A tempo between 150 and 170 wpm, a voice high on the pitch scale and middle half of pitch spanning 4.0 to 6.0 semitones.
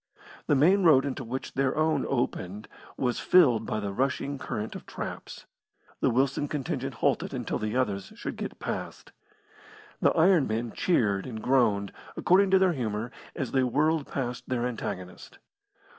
No: average, 160 wpm; low, 130 Hz; average, 4.9 semitones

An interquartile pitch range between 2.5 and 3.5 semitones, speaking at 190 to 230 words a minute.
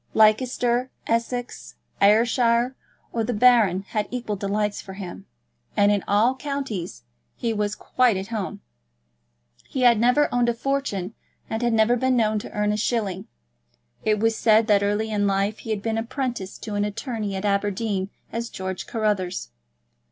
No: average, 2.8 semitones; average, 160 wpm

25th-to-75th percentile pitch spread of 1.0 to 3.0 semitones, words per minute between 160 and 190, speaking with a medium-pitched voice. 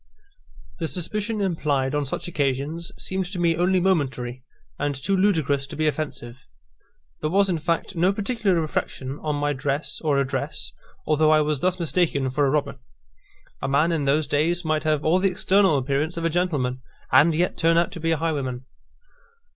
No: average, 3.7 semitones; average, 180 wpm; medium, 155 Hz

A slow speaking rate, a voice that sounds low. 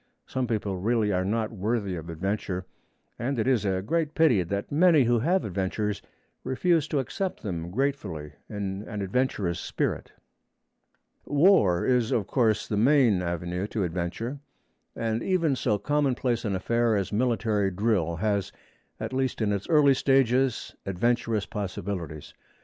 No: average, 145 wpm; low, 110 Hz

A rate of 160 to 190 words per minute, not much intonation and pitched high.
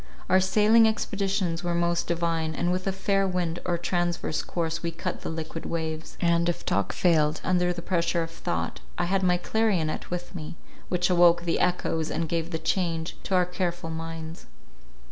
No: average, 185 wpm; narrow, 1.8 semitones; medium, 175 Hz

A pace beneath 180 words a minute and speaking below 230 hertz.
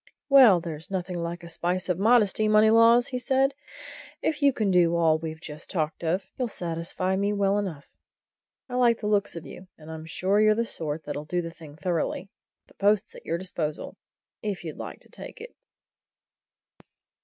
No: average, 185 wpm; medium, 185 Hz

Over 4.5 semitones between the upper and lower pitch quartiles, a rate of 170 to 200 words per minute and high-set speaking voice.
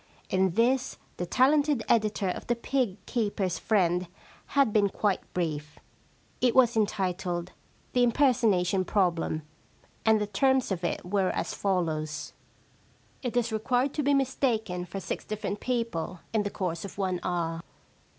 No: average, 5.2 semitones; average, 155 wpm; high, 205 Hz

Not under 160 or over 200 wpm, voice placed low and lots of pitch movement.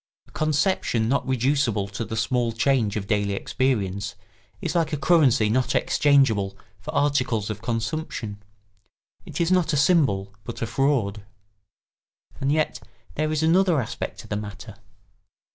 No: average, 145 wpm; low, 125 Hz; wide, 5.7 semitones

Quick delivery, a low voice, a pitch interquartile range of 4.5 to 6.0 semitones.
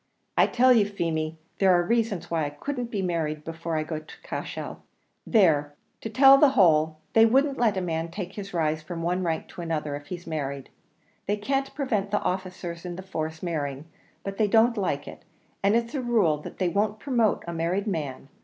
No: fast, 210 wpm; medium, 180 Hz; average, 5.3 semitones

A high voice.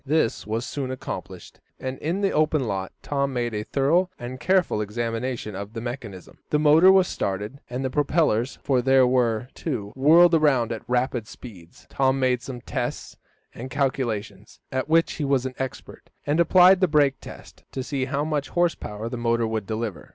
No: low, 130 Hz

